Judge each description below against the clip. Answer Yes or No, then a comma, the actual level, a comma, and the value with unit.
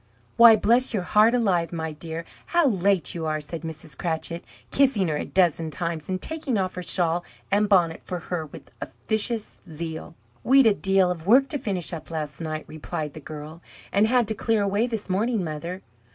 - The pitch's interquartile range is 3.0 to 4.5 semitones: No, average, 5.1 semitones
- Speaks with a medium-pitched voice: Yes, medium, 180 Hz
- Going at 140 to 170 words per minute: No, average, 195 wpm